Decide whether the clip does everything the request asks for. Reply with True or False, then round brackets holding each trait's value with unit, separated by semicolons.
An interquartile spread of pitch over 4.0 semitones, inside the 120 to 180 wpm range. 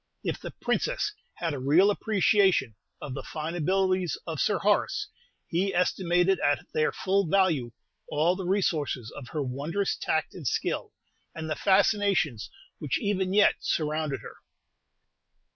True (4.5 semitones; 145 wpm)